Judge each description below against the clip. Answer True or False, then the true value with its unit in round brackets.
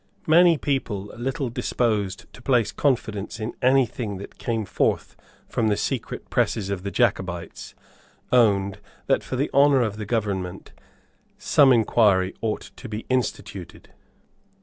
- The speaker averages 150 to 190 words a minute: False (140 wpm)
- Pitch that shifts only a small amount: False (4.2 semitones)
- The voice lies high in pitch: False (110 Hz)